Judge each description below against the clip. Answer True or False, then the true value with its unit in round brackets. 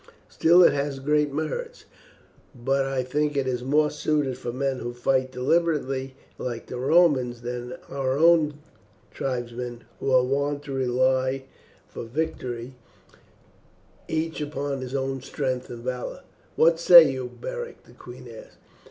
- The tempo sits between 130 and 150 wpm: True (145 wpm)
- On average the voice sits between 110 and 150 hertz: True (135 Hz)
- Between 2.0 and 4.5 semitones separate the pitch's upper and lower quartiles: True (2.9 semitones)